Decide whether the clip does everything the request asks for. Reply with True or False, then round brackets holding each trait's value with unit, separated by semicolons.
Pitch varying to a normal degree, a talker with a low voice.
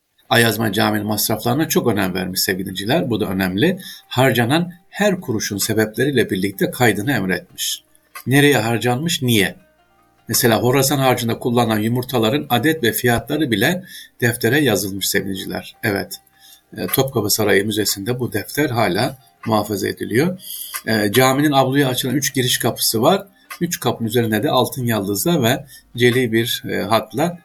True (4.1 semitones; 120 Hz)